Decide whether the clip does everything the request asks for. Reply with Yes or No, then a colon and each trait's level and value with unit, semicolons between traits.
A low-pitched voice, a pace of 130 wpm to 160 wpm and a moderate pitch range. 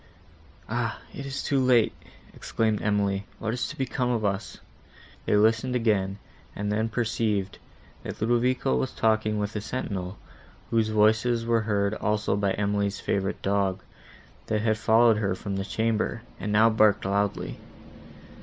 No: low, 110 Hz; average, 150 wpm; narrow, 2.2 semitones